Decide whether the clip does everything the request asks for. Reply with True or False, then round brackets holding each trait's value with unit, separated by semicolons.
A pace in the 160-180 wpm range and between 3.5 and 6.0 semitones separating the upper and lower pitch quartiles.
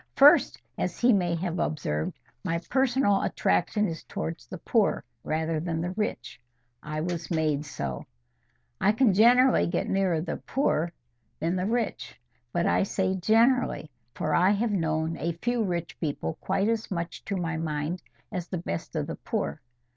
True (165 wpm; 4.7 semitones)